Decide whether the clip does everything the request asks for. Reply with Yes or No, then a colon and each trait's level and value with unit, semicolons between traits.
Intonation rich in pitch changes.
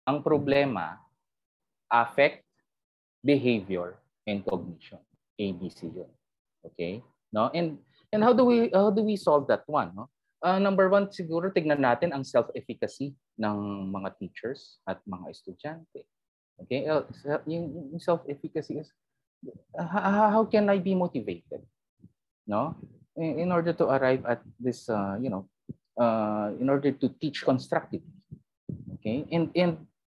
Yes: wide, 6.4 semitones